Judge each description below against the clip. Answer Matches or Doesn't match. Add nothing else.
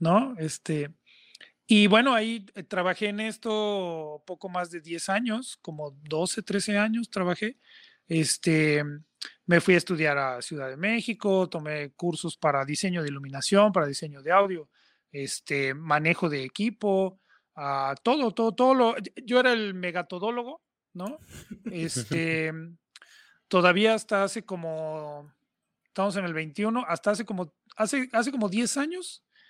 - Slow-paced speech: Doesn't match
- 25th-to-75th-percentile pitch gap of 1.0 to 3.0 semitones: Doesn't match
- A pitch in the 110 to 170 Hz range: Doesn't match